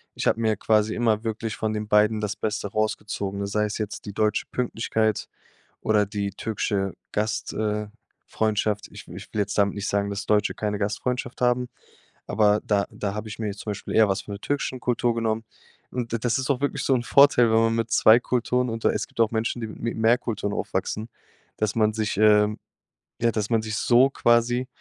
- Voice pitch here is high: No, low, 110 Hz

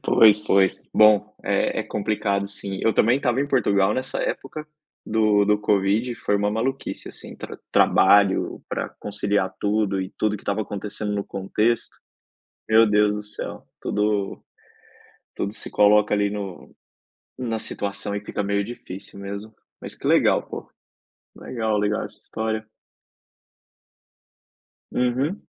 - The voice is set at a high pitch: No, low, 105 Hz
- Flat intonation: Yes, narrow, 1.5 semitones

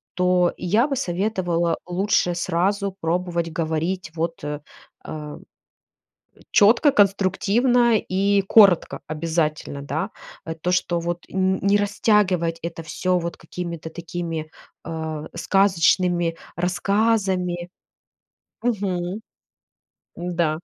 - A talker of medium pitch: Yes, medium, 180 Hz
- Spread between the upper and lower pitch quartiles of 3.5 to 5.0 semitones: No, average, 3.0 semitones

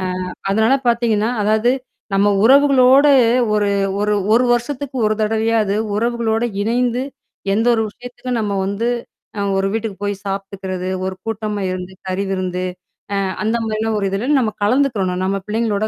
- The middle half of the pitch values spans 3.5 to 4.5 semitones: No, average, 3.0 semitones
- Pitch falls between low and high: No, high, 215 Hz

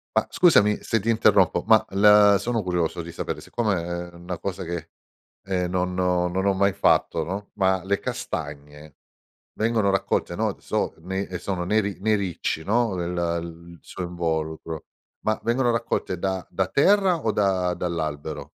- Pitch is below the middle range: Yes, very low, 95 Hz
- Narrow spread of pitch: No, average, 3.3 semitones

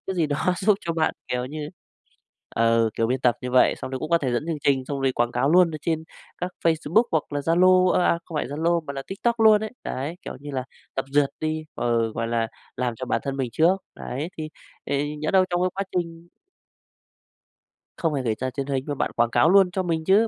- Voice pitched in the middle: Yes, medium, 150 Hz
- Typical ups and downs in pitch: Yes, average, 4.6 semitones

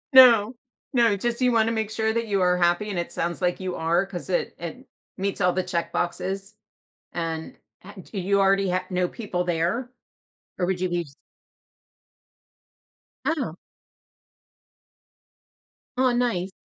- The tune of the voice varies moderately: Yes, average, 3.8 semitones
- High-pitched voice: Yes, high, 195 Hz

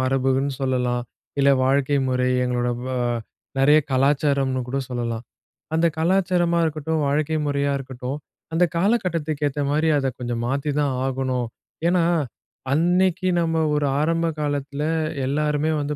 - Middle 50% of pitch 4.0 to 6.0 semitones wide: No, average, 3.3 semitones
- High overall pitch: No, medium, 145 Hz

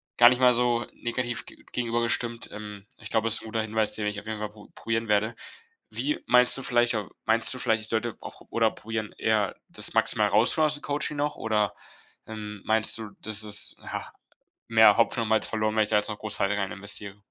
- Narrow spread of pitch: Yes, narrow, 1.9 semitones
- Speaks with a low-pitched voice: Yes, low, 110 Hz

